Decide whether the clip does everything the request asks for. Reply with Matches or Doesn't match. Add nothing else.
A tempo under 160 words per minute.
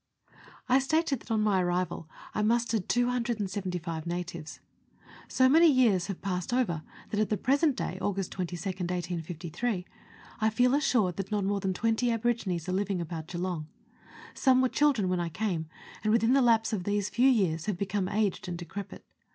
Doesn't match